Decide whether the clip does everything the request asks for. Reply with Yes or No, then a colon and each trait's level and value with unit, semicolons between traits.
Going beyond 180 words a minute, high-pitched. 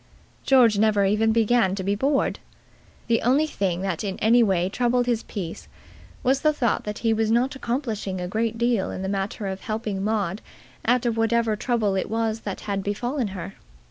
Yes: average, 190 wpm; high, 220 Hz